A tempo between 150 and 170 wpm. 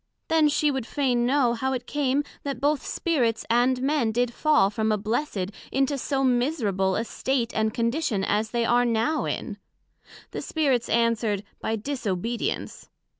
Yes: average, 160 wpm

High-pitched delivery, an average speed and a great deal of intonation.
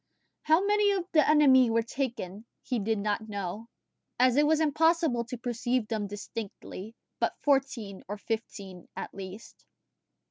Yes: high, 235 Hz; average, 145 wpm; wide, 5.8 semitones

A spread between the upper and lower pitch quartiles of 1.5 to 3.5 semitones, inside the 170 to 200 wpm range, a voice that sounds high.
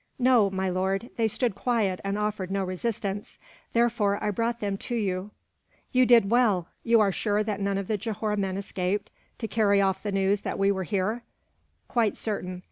Yes: average, 2.7 semitones; average, 190 wpm; high, 205 Hz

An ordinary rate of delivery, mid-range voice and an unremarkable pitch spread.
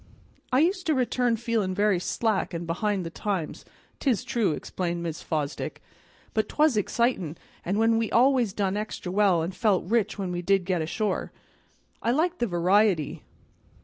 No: average, 160 wpm; high, 205 Hz; average, 4.8 semitones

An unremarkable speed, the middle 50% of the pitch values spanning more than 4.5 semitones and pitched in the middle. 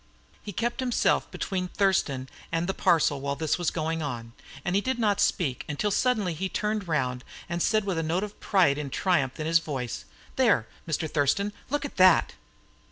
Yes: average, 190 wpm; wide, 5.6 semitones; medium, 175 Hz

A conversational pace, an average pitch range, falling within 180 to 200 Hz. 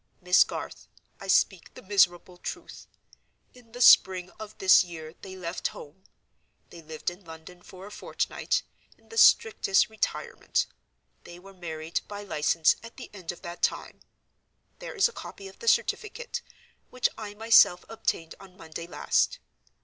Yes: average, 155 wpm; average, 3.9 semitones; medium, 185 Hz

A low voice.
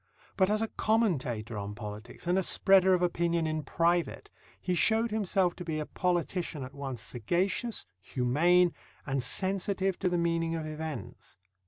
No: medium, 170 Hz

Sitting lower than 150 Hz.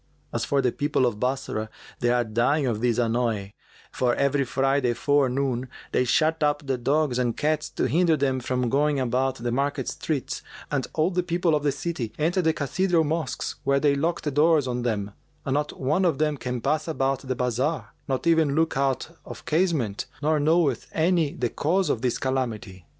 Yes: medium, 140 Hz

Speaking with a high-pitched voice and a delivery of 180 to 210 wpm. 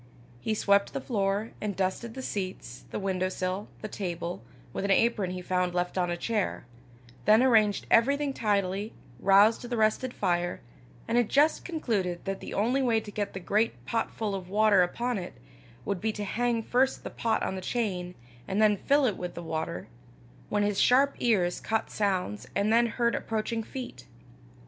Yes: high, 205 Hz; average, 185 wpm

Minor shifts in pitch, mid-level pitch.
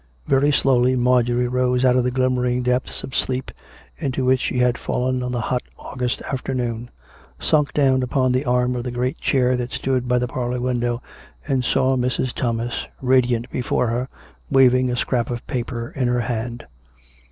No: narrow, 1.0 semitones; low, 125 Hz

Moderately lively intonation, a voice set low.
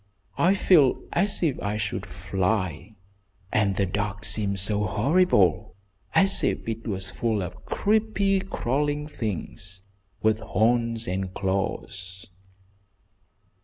No: wide, 6.6 semitones; low, 105 Hz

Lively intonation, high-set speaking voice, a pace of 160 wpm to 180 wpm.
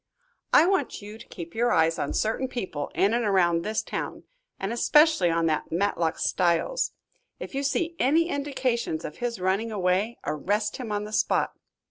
Yes: wide, 5.9 semitones; high, 210 Hz; average, 175 wpm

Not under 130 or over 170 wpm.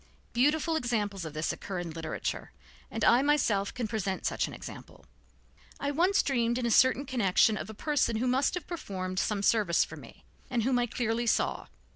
No: average, 190 wpm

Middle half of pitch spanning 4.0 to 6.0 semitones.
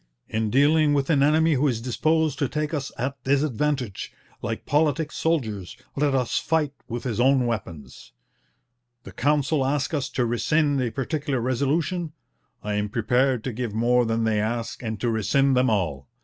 Yes: average, 4.4 semitones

